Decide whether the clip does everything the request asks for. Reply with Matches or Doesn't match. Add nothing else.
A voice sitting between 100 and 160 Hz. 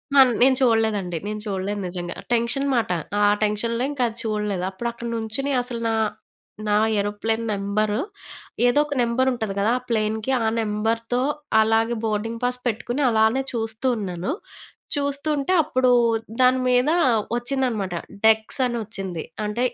Doesn't match